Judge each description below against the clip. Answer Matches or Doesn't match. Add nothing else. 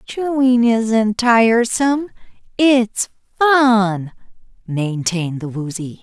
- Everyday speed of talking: Doesn't match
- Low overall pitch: Doesn't match